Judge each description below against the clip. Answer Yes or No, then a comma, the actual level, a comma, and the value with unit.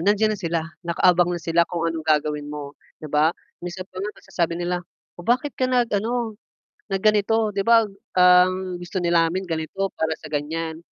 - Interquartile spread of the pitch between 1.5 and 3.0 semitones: No, average, 3.8 semitones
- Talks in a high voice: No, medium, 175 Hz